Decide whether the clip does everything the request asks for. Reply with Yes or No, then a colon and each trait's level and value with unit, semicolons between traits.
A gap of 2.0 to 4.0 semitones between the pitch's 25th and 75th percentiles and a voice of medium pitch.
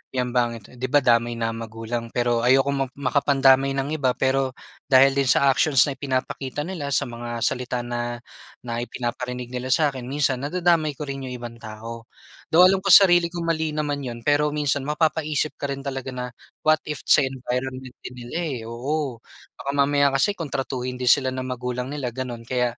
No: average, 2.8 semitones; low, 130 Hz